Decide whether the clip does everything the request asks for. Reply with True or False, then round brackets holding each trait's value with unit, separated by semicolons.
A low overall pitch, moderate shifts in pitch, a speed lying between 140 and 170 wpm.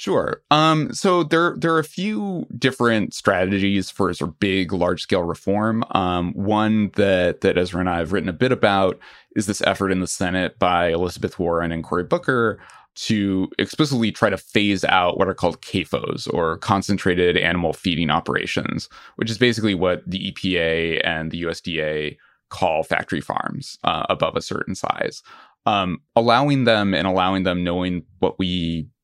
True (95 Hz; 4.0 semitones; 165 wpm)